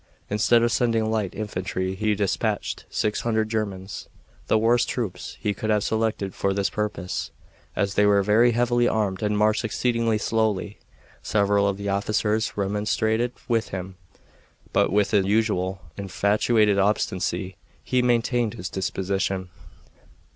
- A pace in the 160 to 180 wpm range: No, average, 140 wpm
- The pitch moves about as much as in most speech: No, narrow, 2.2 semitones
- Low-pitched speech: Yes, low, 105 Hz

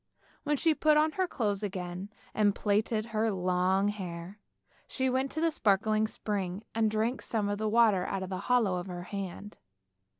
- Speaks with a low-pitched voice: No, high, 210 Hz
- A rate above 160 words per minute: Yes, average, 190 wpm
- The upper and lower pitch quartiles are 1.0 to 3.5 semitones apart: Yes, average, 3.2 semitones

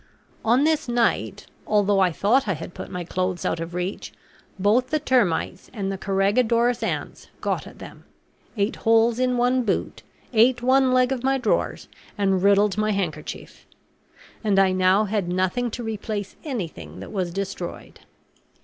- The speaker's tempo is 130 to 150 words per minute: No, average, 160 wpm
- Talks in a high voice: Yes, high, 205 Hz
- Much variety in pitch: No, average, 4.6 semitones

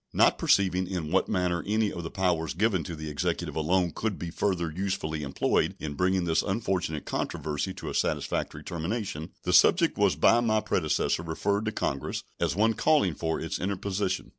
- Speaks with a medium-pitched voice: No, very low, 90 Hz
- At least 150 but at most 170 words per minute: No, average, 180 wpm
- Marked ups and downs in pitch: No, average, 3.8 semitones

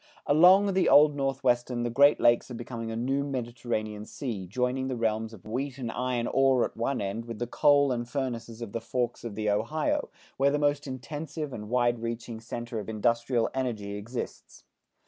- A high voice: No, low, 120 Hz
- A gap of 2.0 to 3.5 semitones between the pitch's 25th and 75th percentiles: Yes, average, 3.0 semitones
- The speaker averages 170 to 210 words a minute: Yes, average, 185 wpm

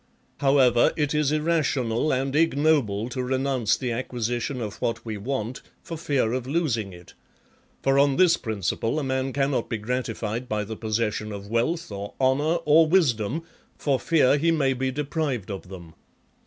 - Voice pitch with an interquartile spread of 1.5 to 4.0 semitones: No, average, 4.6 semitones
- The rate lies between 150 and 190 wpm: Yes, average, 170 wpm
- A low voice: Yes, low, 130 Hz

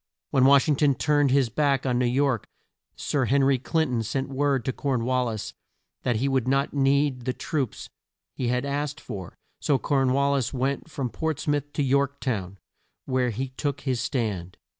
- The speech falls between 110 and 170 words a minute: No, average, 195 wpm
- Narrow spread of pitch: Yes, narrow, 2.1 semitones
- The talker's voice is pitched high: No, low, 135 Hz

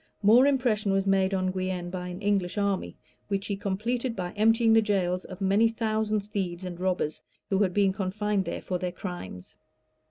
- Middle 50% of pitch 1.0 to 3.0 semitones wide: Yes, narrow, 2.4 semitones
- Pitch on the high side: Yes, high, 195 Hz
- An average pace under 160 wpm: No, average, 185 wpm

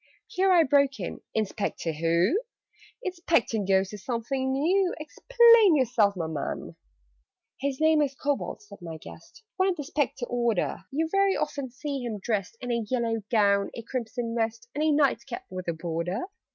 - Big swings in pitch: Yes, wide, 6.5 semitones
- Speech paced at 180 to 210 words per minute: No, average, 170 wpm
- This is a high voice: Yes, high, 245 Hz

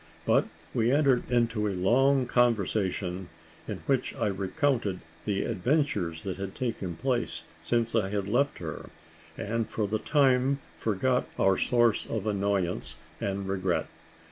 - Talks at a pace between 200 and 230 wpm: No, average, 140 wpm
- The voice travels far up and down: No, average, 4.2 semitones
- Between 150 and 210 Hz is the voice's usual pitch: No, low, 110 Hz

